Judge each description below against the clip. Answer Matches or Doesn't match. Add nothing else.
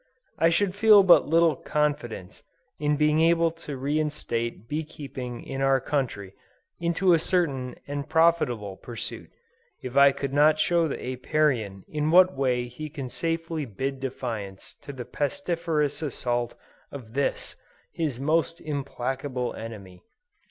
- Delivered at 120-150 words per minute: Matches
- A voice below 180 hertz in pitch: Matches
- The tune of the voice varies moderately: Matches